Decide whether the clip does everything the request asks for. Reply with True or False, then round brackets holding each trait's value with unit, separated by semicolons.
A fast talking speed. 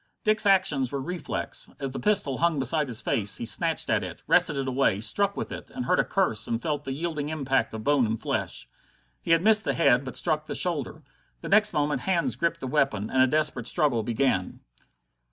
True (210 wpm)